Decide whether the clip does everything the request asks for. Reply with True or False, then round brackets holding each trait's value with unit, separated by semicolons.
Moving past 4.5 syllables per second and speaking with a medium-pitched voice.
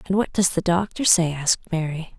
True (5.6 syllables/s; 175 Hz)